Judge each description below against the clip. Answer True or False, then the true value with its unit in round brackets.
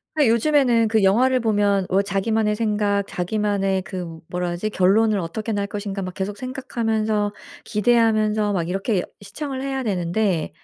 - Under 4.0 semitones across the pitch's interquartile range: True (2.6 semitones)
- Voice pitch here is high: True (210 Hz)